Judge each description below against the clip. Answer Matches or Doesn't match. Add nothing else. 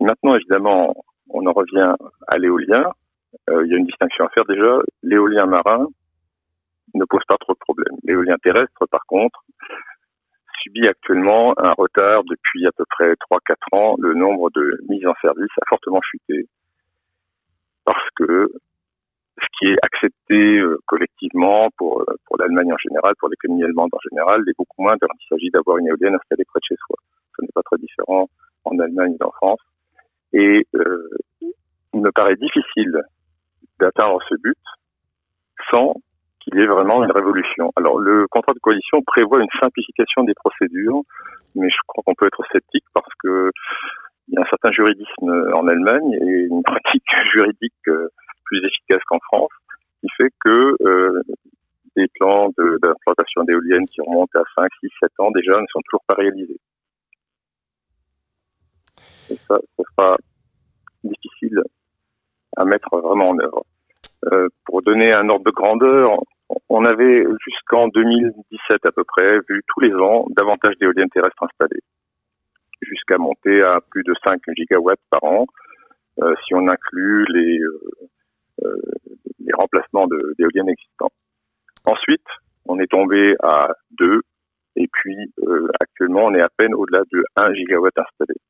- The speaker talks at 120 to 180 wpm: Matches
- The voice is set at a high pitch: Doesn't match